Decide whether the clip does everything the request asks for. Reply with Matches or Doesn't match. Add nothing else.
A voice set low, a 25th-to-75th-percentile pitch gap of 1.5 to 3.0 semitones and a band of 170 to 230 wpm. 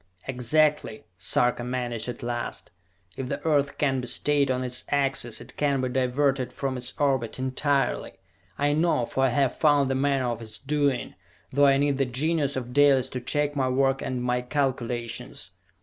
Matches